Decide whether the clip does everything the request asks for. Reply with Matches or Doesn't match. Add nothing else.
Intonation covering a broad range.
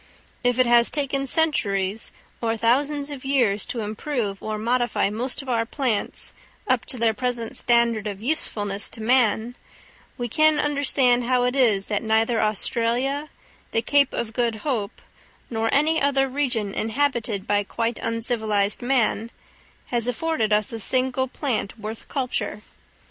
Doesn't match